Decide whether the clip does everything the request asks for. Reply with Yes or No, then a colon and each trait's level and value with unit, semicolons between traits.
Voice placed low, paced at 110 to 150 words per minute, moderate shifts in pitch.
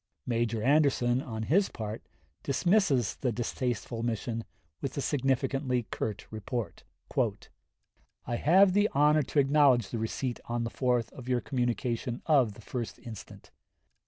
Yes: low, 125 Hz; slow, 135 wpm; average, 3.2 semitones